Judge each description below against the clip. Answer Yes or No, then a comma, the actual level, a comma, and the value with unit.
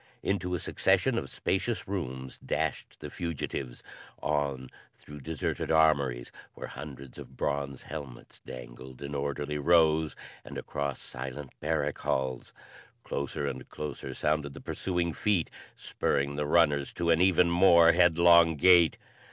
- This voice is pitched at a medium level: No, very low, 75 Hz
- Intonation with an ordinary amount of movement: Yes, average, 3.5 semitones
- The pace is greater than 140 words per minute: No, slow, 135 wpm